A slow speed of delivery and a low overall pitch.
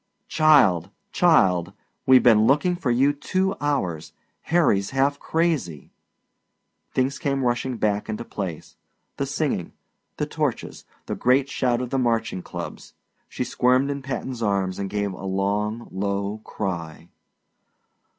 Yes: slow, 130 wpm; low, 120 Hz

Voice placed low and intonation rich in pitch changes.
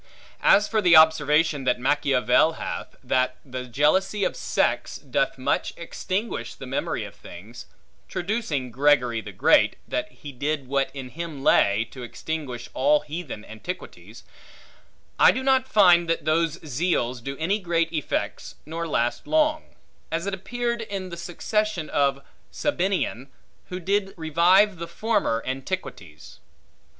No: medium, 160 Hz; wide, 5.8 semitones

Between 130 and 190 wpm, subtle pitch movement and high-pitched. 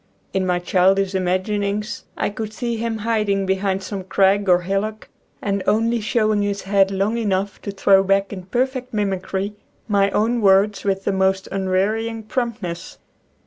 Yes: average, 165 wpm; narrow, 2.0 semitones; high, 200 Hz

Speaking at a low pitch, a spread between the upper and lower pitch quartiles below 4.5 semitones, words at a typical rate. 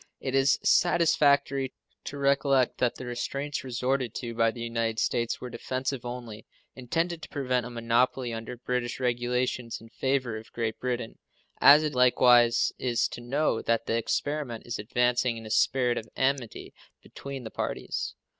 Yes: low, 125 Hz; narrow, 2.4 semitones; average, 160 wpm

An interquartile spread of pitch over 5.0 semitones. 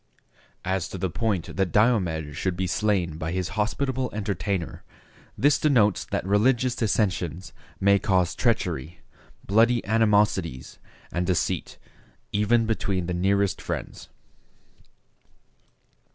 No: average, 3.8 semitones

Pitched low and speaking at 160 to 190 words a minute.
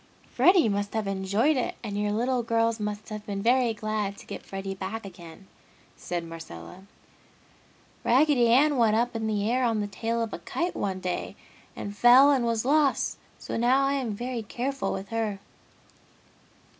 No: high, 225 Hz; average, 175 wpm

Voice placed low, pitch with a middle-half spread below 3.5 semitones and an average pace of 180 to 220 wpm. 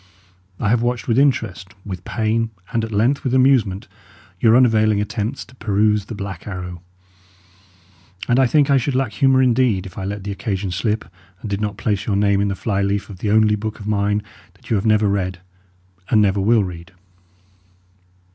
Yes: low, 105 Hz; average, 2.8 semitones; average, 195 wpm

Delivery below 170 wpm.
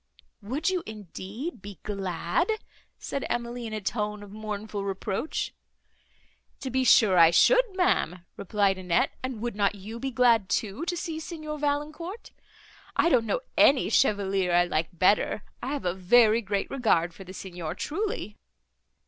Yes: average, 155 wpm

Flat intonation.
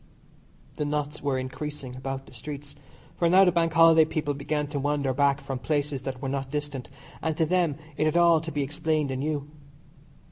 Yes: narrow, 2.3 semitones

